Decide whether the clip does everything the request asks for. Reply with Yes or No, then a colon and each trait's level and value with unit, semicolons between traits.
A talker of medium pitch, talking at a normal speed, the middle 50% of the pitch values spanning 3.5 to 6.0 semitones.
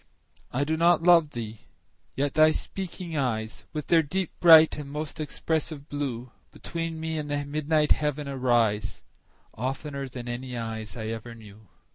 Yes: medium, 145 Hz; average, 155 wpm; average, 4.7 semitones